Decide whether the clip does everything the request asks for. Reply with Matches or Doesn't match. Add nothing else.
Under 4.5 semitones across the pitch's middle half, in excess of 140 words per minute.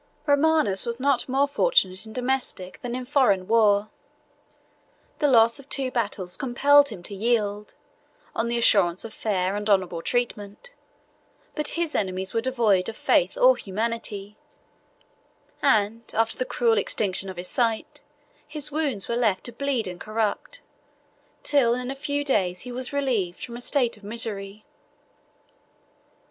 Doesn't match